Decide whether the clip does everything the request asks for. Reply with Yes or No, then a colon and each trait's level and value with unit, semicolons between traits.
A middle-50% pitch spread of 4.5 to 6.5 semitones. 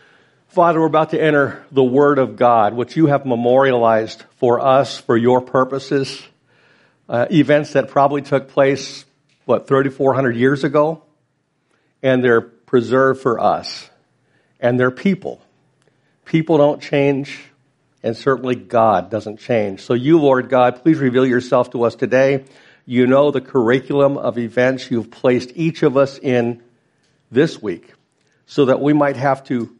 No: narrow, 2.5 semitones